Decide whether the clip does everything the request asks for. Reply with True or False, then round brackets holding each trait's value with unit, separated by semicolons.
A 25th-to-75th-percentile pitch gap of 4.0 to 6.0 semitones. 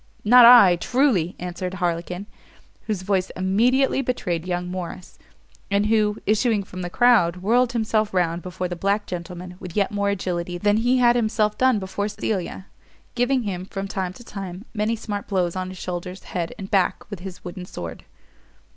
False (3.3 semitones)